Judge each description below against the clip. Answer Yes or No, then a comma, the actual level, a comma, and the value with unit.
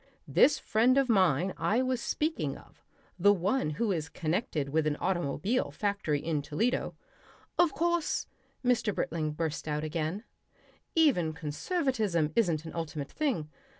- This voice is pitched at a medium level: Yes, medium, 180 Hz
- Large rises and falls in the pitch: Yes, wide, 7.9 semitones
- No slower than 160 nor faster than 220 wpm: No, average, 145 wpm